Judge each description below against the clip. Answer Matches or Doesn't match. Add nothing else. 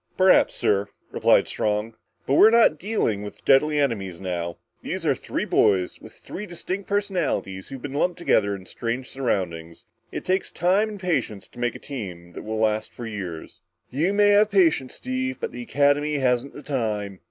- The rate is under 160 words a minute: Doesn't match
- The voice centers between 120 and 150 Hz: Matches